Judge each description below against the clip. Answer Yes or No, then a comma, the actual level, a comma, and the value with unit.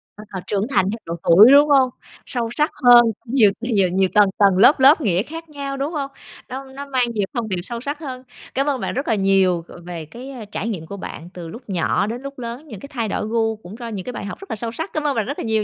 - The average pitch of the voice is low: No, high, 230 Hz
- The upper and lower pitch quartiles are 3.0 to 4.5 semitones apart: No, wide, 5.4 semitones